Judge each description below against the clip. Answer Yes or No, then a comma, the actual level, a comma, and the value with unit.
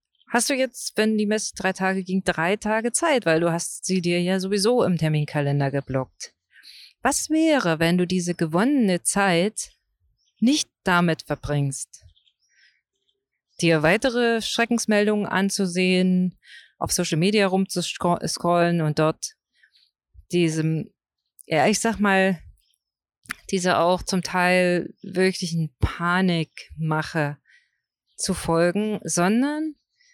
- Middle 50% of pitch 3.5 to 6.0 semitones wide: Yes, average, 4.2 semitones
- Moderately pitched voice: Yes, medium, 180 Hz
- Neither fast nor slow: No, slow, 110 wpm